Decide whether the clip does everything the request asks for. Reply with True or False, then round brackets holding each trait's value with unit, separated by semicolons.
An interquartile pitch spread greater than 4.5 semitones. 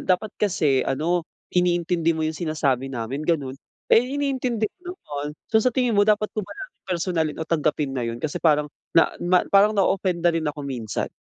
True (5.5 semitones)